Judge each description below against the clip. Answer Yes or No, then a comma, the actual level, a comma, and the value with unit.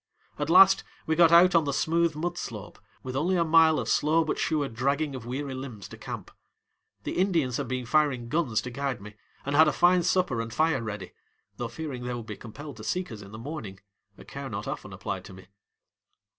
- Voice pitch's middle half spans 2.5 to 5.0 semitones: No, wide, 5.6 semitones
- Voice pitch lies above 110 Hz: Yes, medium, 140 Hz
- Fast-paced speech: Yes, fast, 220 wpm